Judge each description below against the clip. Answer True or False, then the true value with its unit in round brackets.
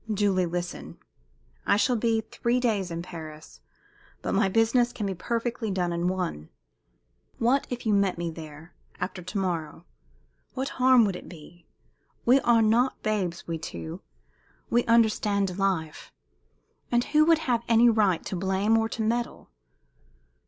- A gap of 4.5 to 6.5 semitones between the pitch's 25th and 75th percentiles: True (5.0 semitones)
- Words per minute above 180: False (150 wpm)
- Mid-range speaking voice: False (200 Hz)